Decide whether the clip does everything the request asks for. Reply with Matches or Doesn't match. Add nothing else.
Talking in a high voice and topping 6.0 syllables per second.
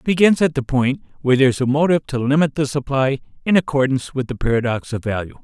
Doesn't match